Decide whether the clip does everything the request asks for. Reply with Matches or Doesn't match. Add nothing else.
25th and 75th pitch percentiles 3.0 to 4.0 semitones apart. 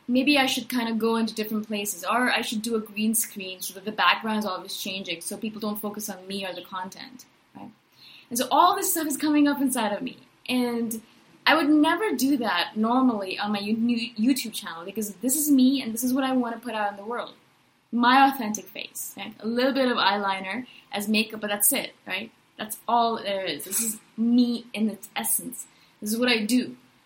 Matches